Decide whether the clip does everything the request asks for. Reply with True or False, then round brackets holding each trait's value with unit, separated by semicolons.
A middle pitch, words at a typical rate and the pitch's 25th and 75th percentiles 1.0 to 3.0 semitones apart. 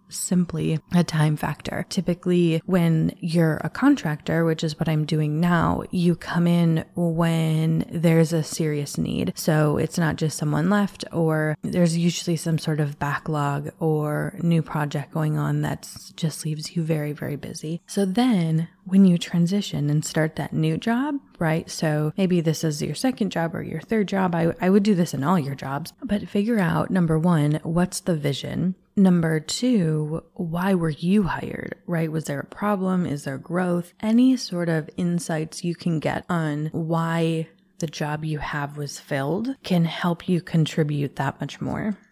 True (165 Hz; 175 wpm; 2.7 semitones)